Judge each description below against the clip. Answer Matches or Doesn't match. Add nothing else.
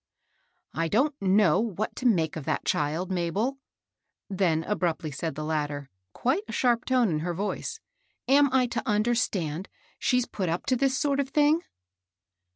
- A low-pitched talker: Doesn't match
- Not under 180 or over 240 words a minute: Doesn't match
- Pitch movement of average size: Doesn't match